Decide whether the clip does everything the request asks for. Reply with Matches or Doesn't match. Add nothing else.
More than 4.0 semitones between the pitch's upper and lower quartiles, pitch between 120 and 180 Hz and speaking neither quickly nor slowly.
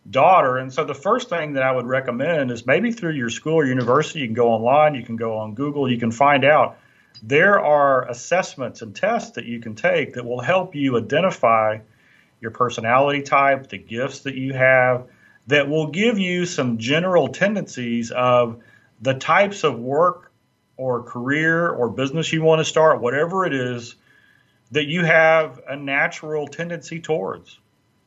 Matches